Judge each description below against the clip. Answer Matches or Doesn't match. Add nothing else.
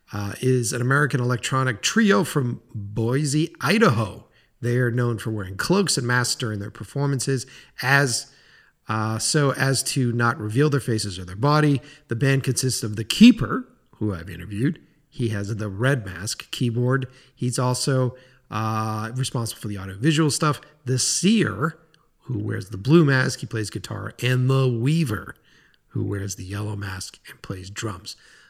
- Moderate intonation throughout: Matches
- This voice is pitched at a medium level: Doesn't match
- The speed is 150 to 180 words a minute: Matches